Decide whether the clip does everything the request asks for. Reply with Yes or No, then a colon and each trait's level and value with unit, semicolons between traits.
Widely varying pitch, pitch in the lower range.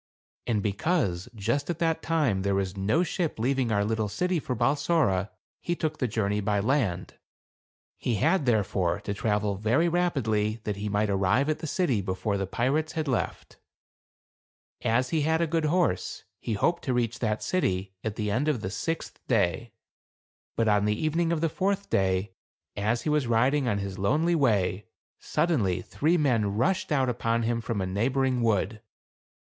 Yes: wide, 6.9 semitones; low, 115 Hz